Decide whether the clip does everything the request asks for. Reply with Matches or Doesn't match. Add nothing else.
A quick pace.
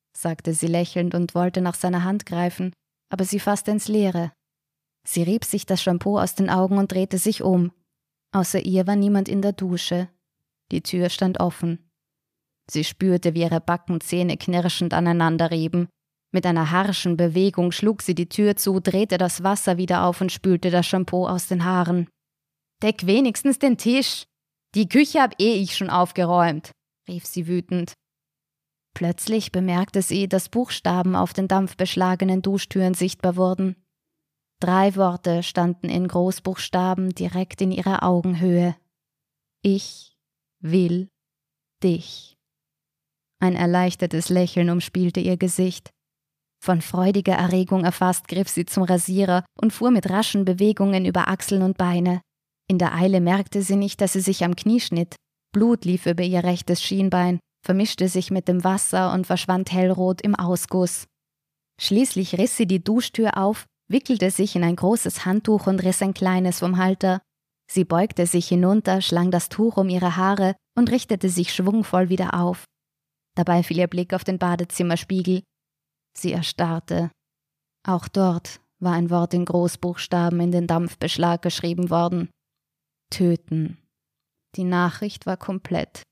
Doesn't match